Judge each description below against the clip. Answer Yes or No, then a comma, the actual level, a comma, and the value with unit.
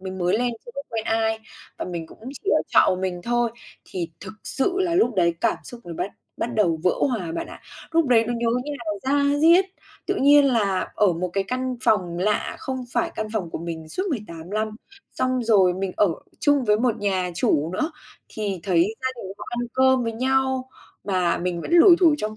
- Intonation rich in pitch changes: Yes, wide, 5.9 semitones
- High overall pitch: Yes, high, 220 Hz